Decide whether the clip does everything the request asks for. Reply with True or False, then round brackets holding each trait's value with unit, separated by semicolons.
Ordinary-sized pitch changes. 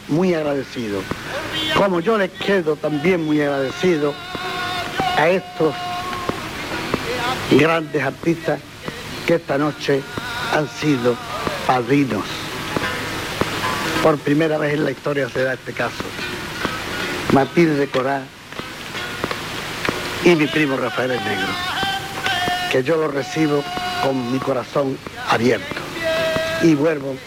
True (4.7 semitones)